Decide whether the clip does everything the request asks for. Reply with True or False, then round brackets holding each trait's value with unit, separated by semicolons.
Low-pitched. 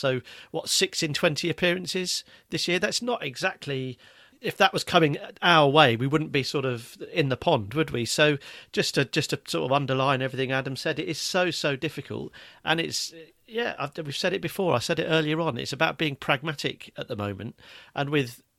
False (150 Hz)